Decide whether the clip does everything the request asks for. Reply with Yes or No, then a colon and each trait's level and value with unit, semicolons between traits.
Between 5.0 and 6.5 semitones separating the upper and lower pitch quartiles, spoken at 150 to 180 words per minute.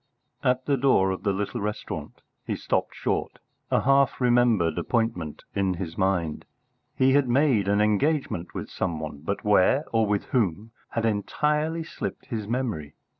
Yes: wide, 5.4 semitones; average, 160 wpm